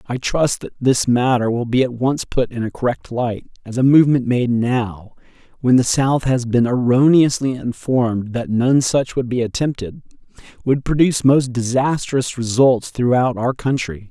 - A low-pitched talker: Yes, low, 125 Hz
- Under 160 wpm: No, average, 170 wpm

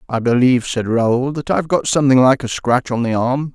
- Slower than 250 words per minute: No, fast, 255 wpm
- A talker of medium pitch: No, low, 130 Hz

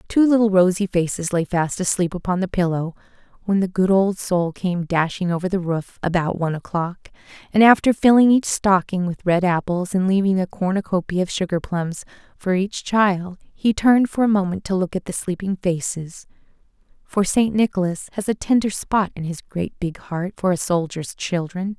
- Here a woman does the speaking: Yes, female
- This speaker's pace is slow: No, average, 185 wpm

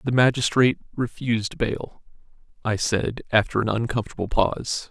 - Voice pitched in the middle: No, low, 115 Hz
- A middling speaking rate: No, slow, 120 wpm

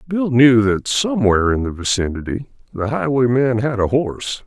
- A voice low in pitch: Yes, low, 120 Hz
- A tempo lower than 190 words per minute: Yes, average, 160 wpm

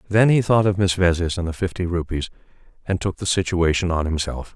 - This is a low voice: Yes, very low, 90 Hz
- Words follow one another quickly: Yes, fast, 210 wpm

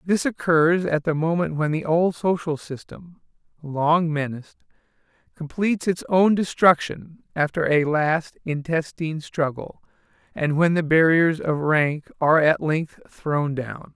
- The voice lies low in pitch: No, medium, 160 Hz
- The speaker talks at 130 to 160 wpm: Yes, average, 140 wpm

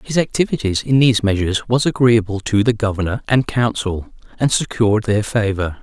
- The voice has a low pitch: Yes, low, 110 Hz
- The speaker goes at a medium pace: Yes, average, 165 wpm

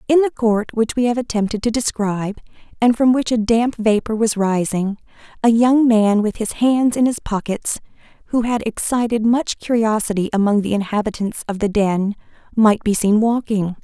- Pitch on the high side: Yes, high, 220 Hz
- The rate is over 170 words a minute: Yes, average, 180 wpm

